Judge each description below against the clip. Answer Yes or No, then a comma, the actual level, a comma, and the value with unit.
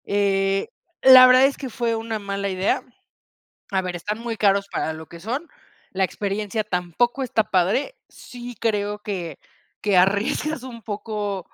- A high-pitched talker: Yes, high, 205 Hz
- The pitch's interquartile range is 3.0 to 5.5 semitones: Yes, average, 3.3 semitones